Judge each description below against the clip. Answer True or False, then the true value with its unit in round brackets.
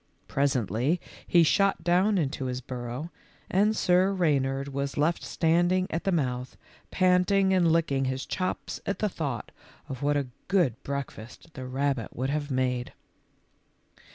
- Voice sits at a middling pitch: True (145 Hz)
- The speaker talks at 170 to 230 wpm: False (145 wpm)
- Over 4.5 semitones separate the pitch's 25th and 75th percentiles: True (5.4 semitones)